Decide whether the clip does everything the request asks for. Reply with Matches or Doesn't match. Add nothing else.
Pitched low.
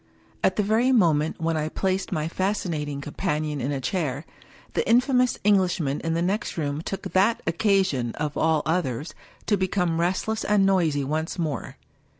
Doesn't match